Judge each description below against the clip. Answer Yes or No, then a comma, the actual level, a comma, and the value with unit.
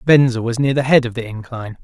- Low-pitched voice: Yes, low, 125 Hz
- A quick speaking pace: Yes, fast, 260 wpm